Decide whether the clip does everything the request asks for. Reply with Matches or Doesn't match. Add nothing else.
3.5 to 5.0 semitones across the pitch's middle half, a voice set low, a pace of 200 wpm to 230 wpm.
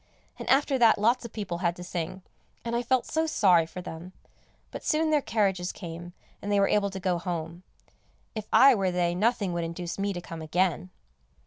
Doesn't match